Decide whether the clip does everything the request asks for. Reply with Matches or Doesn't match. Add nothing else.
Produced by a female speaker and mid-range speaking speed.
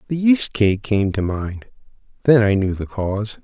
Doesn't match